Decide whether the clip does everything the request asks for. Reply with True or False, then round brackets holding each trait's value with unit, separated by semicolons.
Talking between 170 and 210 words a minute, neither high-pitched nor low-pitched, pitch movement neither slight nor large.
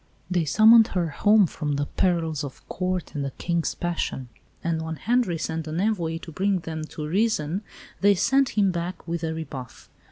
True (185 wpm; 170 Hz; 3.4 semitones)